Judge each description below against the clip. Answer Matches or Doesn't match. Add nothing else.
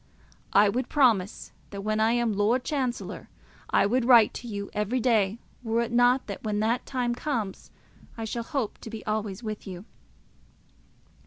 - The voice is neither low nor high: Doesn't match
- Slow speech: Doesn't match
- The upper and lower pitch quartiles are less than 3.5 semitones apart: Matches